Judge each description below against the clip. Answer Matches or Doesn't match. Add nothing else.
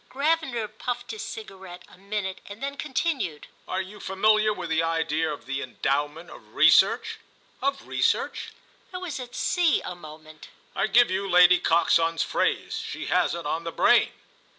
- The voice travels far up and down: Matches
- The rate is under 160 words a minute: Doesn't match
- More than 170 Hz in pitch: Matches